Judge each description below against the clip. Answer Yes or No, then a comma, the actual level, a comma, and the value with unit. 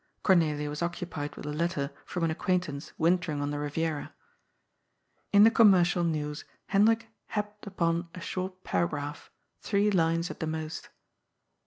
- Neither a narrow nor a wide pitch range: Yes, average, 3.7 semitones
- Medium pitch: Yes, medium, 170 Hz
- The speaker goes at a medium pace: Yes, average, 145 wpm